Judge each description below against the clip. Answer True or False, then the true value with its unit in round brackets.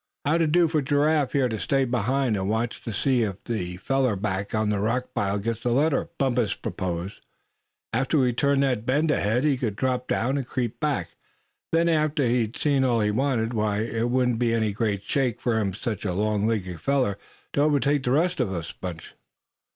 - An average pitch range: True (4.6 semitones)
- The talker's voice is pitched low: True (120 Hz)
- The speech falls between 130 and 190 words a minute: False (200 wpm)